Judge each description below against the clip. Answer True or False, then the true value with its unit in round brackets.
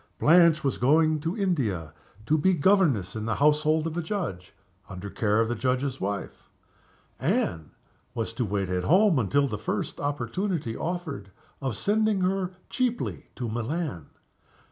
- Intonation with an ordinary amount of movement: False (8.1 semitones)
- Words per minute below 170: True (150 wpm)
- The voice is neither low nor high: True (145 Hz)